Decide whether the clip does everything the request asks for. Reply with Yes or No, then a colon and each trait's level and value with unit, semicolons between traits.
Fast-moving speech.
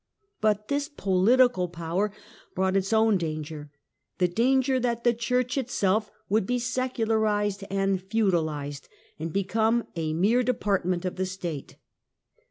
No: slow, 135 wpm